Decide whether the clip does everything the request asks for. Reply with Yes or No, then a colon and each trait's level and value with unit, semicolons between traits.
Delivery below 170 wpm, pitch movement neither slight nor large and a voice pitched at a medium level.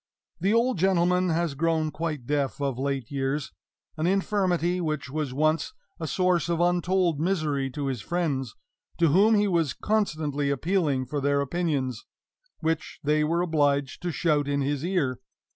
Yes: average, 160 wpm; average, 3.9 semitones; medium, 155 Hz